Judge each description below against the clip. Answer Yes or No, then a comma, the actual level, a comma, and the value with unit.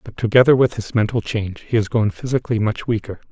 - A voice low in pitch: Yes, low, 115 Hz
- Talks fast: Yes, fast, 215 wpm